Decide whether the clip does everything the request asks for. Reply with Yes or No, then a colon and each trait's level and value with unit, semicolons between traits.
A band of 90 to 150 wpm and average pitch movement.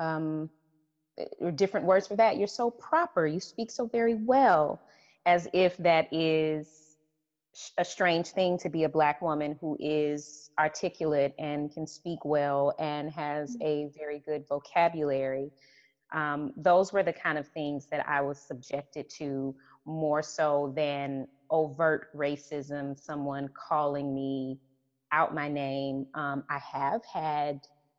No: average, 140 wpm; narrow, 2.3 semitones